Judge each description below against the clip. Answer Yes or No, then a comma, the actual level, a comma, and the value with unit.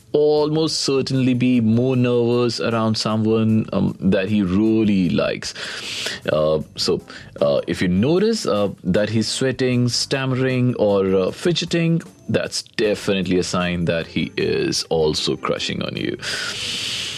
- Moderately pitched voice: No, low, 115 Hz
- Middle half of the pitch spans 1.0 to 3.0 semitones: No, average, 4.6 semitones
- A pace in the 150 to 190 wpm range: No, average, 130 wpm